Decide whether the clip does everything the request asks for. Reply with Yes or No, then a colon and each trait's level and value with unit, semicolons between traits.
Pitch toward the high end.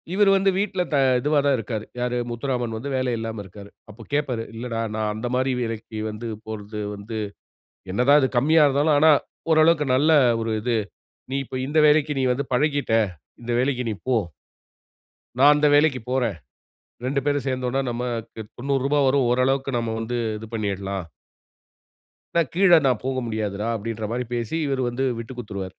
No: low, 125 Hz